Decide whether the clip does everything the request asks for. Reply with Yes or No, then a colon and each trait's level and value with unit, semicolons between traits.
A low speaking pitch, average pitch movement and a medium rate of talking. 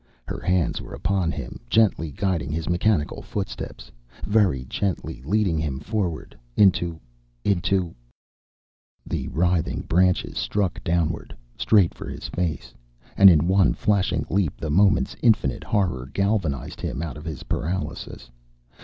No: very low, 90 Hz; average, 4.0 semitones; slow, 130 wpm